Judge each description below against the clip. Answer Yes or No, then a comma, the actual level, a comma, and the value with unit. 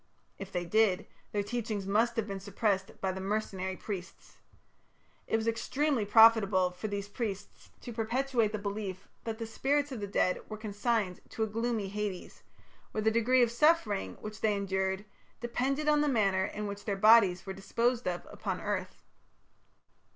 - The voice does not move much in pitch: No, average, 3.0 semitones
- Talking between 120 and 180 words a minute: Yes, average, 170 wpm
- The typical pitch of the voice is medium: No, high, 210 Hz